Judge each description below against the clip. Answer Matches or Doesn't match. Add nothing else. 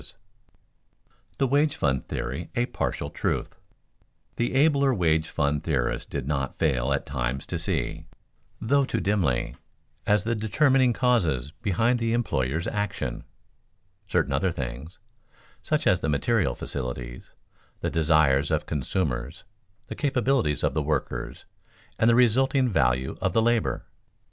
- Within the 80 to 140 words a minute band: Matches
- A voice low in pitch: Matches